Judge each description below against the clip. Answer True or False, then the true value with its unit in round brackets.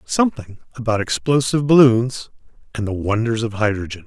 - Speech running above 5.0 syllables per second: True (5.6 syllables/s)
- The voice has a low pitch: True (115 Hz)